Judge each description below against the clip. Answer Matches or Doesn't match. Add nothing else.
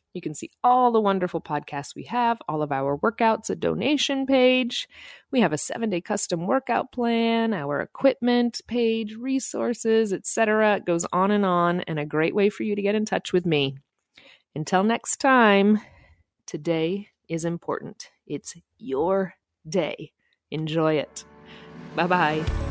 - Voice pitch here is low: Doesn't match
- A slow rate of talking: Doesn't match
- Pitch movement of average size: Doesn't match